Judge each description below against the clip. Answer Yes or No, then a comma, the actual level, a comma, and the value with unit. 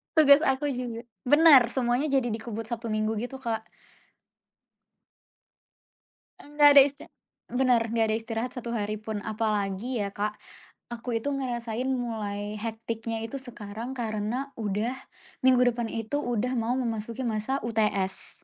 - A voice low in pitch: No, high, 230 Hz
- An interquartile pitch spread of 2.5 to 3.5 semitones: Yes, average, 2.8 semitones